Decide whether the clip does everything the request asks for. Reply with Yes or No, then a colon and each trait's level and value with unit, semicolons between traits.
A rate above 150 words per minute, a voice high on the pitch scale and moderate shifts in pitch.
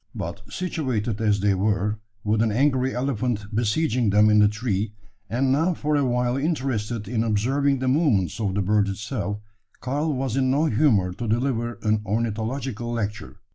No: average, 170 wpm; low, 115 Hz; average, 4.0 semitones